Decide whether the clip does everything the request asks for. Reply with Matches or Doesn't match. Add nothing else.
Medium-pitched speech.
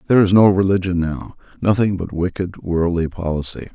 Doesn't match